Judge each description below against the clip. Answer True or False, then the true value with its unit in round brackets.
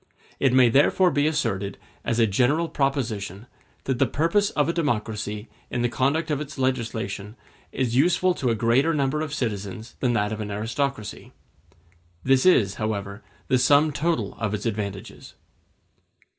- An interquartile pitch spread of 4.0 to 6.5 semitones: True (5.1 semitones)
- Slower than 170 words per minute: True (155 wpm)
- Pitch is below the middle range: True (125 Hz)